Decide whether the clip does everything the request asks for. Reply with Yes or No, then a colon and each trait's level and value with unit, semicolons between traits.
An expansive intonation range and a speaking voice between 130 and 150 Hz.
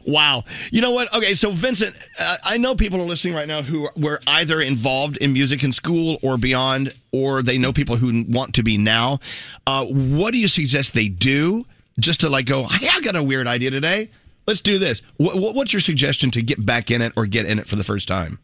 Yes: wide, 5.7 semitones; medium, 140 Hz